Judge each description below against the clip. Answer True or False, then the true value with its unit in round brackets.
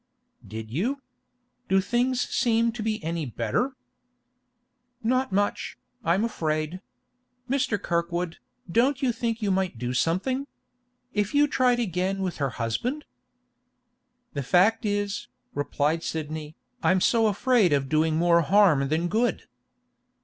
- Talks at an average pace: False (130 wpm)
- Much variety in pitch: True (6.7 semitones)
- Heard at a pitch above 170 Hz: True (190 Hz)